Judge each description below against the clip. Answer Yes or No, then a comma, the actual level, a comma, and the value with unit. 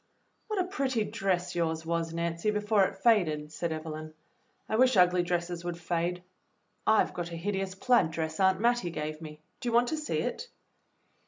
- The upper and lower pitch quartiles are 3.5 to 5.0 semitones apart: Yes, average, 4.5 semitones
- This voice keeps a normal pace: Yes, average, 180 wpm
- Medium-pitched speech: Yes, medium, 180 Hz